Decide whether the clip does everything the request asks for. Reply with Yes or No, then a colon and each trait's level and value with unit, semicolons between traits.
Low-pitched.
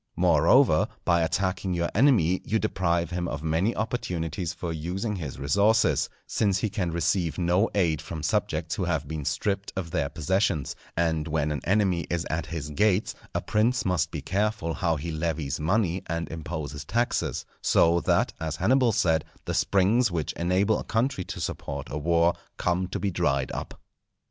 Yes: very low, 85 Hz